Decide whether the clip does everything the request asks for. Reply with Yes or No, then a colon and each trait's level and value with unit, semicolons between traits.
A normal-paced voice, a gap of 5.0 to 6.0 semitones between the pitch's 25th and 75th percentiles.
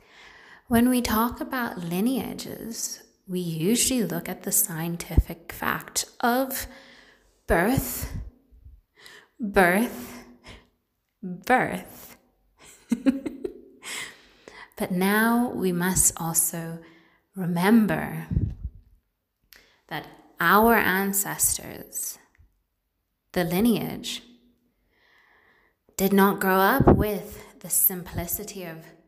No: slow, 70 wpm; wide, 5.5 semitones